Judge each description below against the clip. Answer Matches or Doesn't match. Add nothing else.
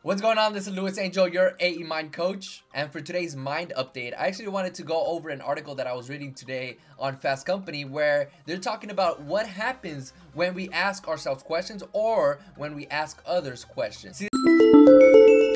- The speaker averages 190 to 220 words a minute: Matches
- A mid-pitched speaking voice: Matches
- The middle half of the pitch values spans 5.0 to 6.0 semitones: Matches